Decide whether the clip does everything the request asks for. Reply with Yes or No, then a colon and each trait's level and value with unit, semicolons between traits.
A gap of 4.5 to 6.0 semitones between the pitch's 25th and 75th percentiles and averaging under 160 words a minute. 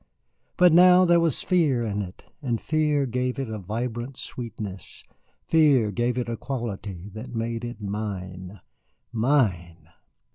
Yes: average, 5.0 semitones; average, 140 wpm